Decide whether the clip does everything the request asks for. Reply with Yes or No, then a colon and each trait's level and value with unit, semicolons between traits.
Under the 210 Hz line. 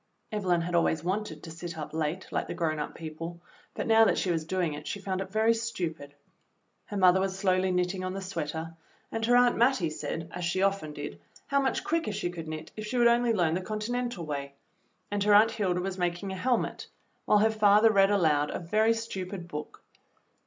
Yes: medium, 185 Hz